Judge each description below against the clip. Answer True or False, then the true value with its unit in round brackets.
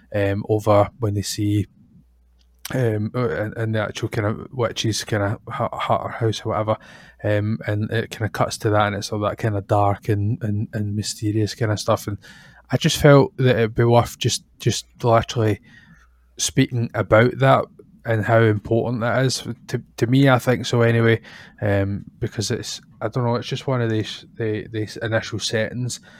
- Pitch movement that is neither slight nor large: False (2.1 semitones)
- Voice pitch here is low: True (110 Hz)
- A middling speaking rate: True (190 wpm)